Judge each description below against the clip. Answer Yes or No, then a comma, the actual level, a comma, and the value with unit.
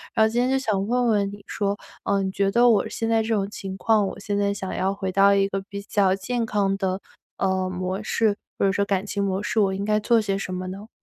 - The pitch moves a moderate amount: No, narrow, 1.8 semitones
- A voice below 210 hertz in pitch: Yes, high, 200 Hz